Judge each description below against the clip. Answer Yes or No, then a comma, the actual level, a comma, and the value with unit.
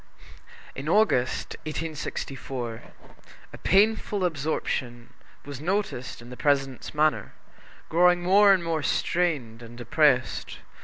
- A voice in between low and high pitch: Yes, medium, 150 Hz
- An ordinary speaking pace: No, slow, 105 wpm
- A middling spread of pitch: No, wide, 6.0 semitones